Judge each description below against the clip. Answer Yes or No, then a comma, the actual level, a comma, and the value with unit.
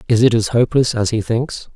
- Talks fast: Yes, fast, 240 wpm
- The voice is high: No, low, 115 Hz